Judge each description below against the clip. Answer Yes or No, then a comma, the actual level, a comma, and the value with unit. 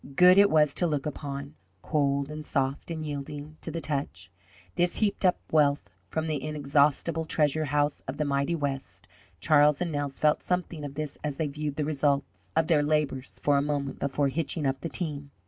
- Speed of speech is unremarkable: Yes, average, 195 wpm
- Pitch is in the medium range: Yes, medium, 150 Hz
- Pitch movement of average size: No, narrow, 1.9 semitones